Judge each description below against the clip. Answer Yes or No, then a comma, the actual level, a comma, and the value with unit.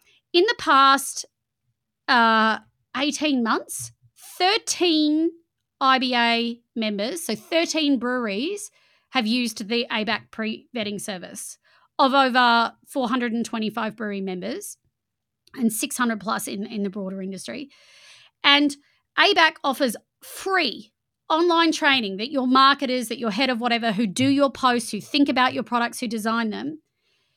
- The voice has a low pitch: No, high, 245 Hz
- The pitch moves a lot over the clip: No, average, 4.2 semitones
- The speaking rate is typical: No, slow, 125 wpm